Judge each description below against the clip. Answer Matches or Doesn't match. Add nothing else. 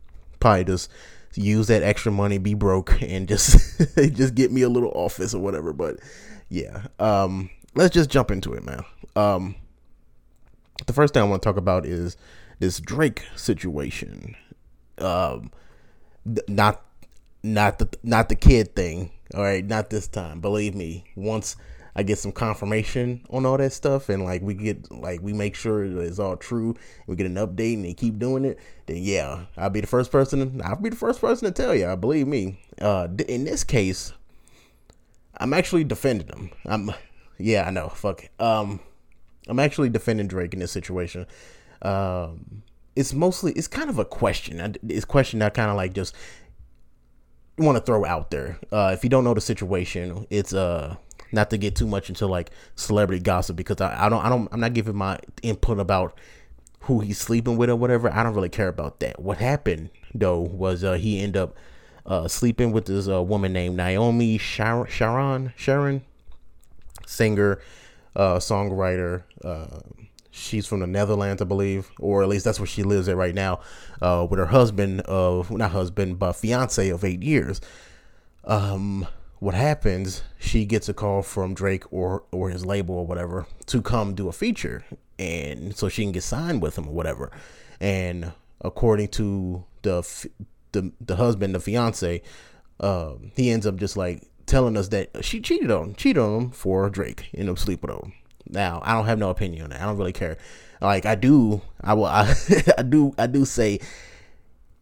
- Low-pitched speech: Matches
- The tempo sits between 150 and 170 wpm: Doesn't match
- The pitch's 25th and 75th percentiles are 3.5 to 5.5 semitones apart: Matches